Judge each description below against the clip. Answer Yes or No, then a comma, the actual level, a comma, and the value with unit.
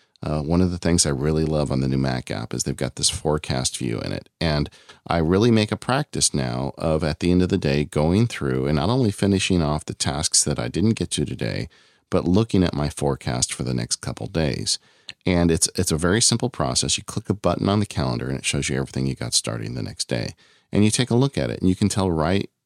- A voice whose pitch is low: Yes, very low, 85 Hz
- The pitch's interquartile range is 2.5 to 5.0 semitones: No, wide, 5.6 semitones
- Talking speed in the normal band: No, fast, 260 wpm